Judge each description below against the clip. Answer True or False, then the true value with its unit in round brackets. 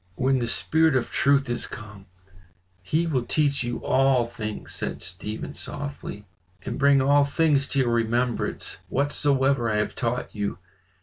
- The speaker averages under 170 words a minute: True (150 wpm)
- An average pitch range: True (3.3 semitones)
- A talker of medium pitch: False (130 Hz)